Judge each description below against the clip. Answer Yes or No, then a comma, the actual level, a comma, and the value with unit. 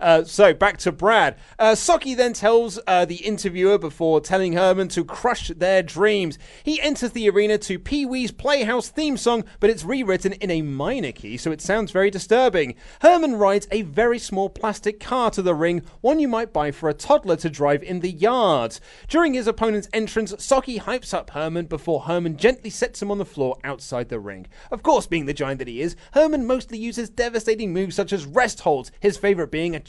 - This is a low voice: No, high, 200 Hz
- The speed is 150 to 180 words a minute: No, fast, 205 wpm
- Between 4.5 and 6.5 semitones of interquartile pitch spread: Yes, wide, 5.4 semitones